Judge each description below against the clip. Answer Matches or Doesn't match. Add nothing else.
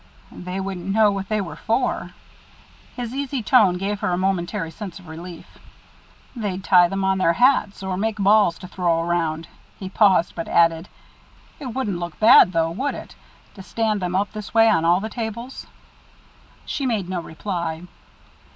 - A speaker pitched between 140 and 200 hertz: Matches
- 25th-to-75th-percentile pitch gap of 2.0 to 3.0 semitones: Doesn't match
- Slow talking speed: Doesn't match